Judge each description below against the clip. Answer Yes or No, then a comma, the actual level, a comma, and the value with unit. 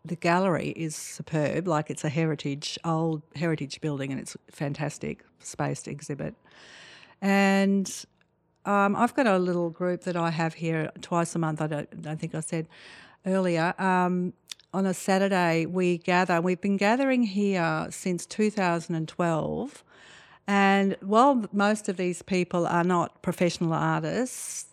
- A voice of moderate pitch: Yes, medium, 175 Hz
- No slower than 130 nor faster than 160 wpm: Yes, average, 150 wpm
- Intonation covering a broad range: No, average, 3.1 semitones